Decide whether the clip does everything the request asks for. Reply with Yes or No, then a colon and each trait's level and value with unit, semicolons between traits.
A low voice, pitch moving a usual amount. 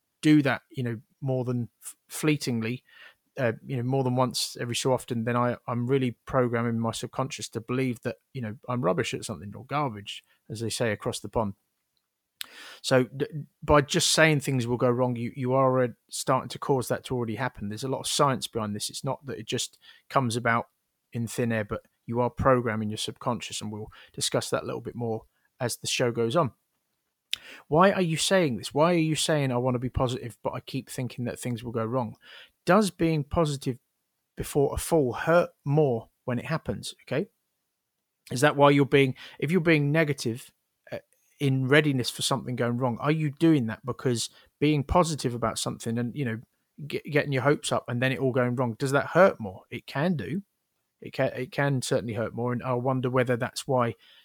Yes: low, 125 Hz; average, 3.4 semitones